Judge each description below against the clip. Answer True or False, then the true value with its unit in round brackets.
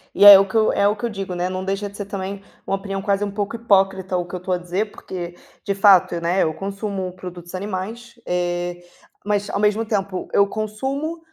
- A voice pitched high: True (195 Hz)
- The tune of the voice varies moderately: False (2.1 semitones)